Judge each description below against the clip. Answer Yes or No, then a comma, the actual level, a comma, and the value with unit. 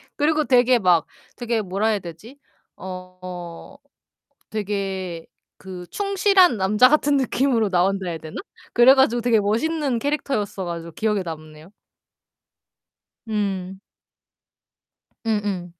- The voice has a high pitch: Yes, high, 205 Hz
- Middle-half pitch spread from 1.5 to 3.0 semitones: No, wide, 5.4 semitones